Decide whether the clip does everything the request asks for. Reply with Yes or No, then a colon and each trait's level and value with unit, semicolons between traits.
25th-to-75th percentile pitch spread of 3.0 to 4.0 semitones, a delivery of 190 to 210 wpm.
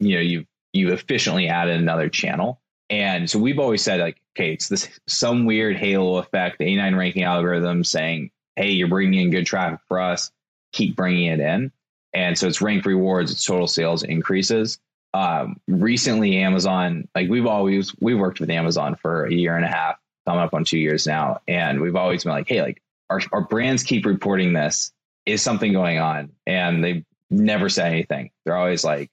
No: narrow, 2.4 semitones; average, 195 wpm